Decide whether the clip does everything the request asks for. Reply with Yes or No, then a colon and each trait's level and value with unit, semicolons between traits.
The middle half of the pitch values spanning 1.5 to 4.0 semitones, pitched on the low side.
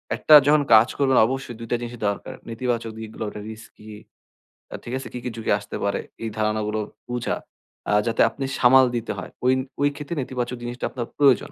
Yes: average, 2.7 semitones; low, 120 Hz